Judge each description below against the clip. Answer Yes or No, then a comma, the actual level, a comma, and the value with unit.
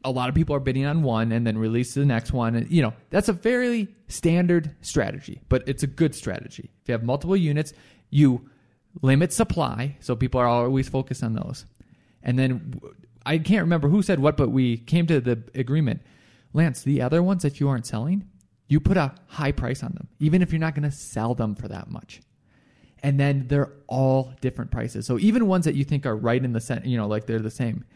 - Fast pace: Yes, fast, 230 wpm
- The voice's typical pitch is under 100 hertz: No, low, 135 Hz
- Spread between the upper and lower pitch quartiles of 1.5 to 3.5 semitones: No, average, 4.4 semitones